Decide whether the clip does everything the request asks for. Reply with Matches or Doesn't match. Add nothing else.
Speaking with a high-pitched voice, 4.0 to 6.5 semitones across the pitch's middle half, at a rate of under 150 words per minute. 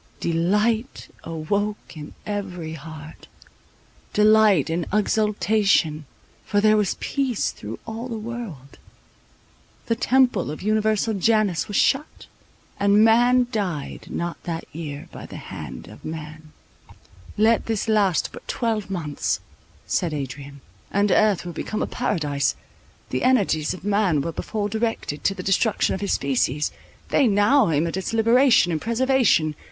Matches